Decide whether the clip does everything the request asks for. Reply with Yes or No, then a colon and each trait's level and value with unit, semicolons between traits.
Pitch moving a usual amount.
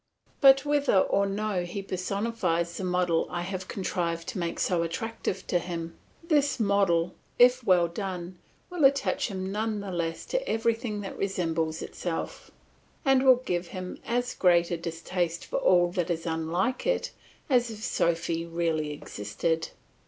Yes: average, 4.7 semitones